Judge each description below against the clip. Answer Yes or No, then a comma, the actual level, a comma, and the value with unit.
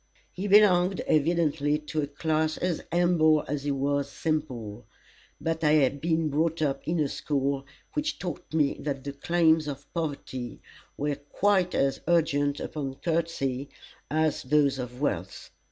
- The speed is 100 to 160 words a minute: Yes, average, 150 wpm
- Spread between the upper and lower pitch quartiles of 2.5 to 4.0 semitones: Yes, average, 2.8 semitones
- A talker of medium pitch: Yes, medium, 150 Hz